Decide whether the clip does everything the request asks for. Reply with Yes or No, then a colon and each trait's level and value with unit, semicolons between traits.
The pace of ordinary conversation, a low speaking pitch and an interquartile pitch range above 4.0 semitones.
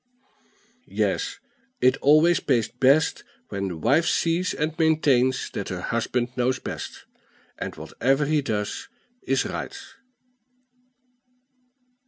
No: slow, 110 wpm; low, 130 Hz; average, 4.5 semitones